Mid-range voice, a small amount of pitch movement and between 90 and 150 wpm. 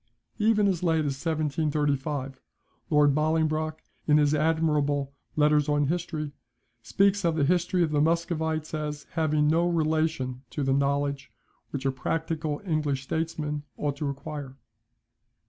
Yes: medium, 150 Hz; narrow, 2.0 semitones; slow, 135 wpm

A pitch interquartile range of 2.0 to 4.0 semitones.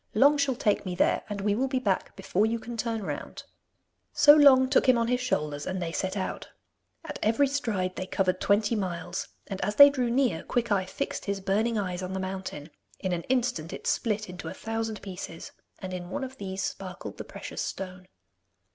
No: average, 4.8 semitones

